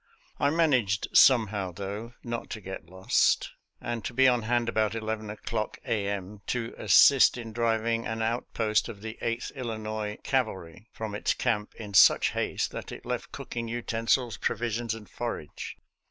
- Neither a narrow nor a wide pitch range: No, narrow, 2.2 semitones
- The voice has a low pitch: Yes, low, 110 Hz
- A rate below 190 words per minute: Yes, average, 160 wpm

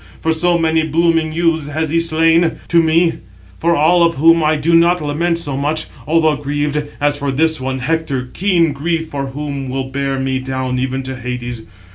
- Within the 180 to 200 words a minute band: Yes, average, 190 wpm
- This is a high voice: No, medium, 155 Hz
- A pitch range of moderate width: Yes, average, 3.2 semitones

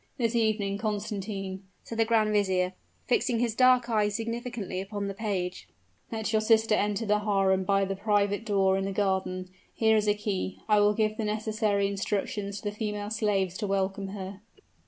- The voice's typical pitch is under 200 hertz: No, high, 205 Hz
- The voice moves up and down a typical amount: No, narrow, 2.0 semitones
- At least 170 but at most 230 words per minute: Yes, average, 180 wpm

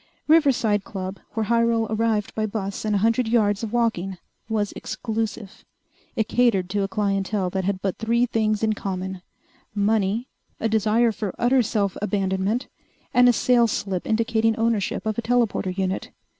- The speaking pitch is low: No, high, 215 Hz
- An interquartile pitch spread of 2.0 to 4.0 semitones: Yes, narrow, 2.6 semitones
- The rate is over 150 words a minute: Yes, average, 160 wpm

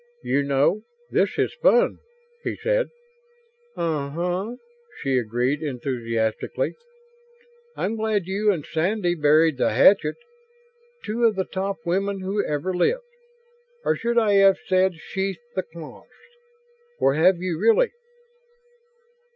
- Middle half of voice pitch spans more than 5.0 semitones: Yes, wide, 5.6 semitones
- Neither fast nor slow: No, slow, 125 wpm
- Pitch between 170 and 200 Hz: Yes, medium, 185 Hz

